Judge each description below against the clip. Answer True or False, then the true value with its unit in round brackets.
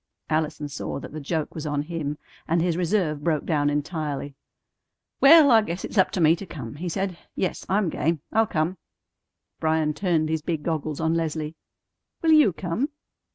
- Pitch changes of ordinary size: True (3.0 semitones)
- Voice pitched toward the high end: False (160 Hz)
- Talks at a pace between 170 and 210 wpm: True (180 wpm)